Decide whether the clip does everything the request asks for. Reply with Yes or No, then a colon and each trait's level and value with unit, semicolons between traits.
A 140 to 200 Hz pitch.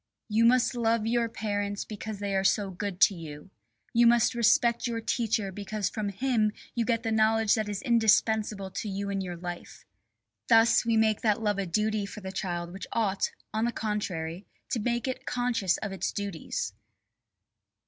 No: high, 215 Hz